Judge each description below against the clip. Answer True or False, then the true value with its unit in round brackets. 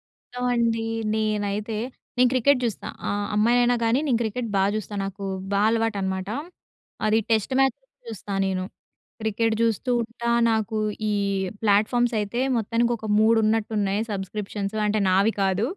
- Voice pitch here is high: True (220 Hz)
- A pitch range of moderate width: False (2.3 semitones)